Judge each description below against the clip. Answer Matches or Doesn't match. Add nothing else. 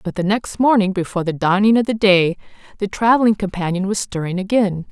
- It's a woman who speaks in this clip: Matches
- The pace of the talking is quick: Doesn't match